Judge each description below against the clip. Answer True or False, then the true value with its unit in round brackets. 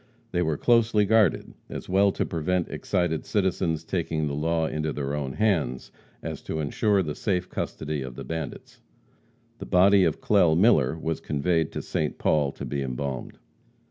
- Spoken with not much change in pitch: False (4.1 semitones)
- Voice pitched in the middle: False (80 Hz)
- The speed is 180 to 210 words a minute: False (170 wpm)